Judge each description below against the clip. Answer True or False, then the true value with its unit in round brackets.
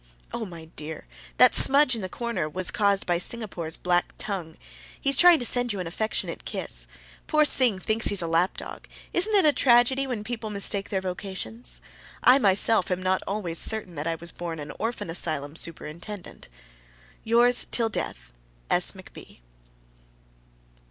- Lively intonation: True (5.7 semitones)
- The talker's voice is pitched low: False (200 Hz)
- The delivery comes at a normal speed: True (165 wpm)